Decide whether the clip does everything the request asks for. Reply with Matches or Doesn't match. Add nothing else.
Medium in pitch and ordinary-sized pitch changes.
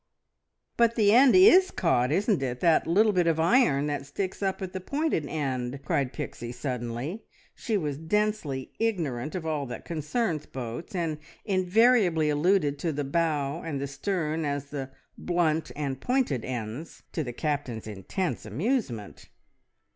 Doesn't match